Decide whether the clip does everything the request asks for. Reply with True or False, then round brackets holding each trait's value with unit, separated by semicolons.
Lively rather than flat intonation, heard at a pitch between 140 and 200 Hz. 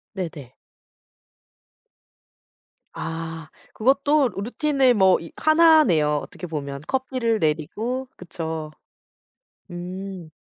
True (8.2 semitones; 185 Hz)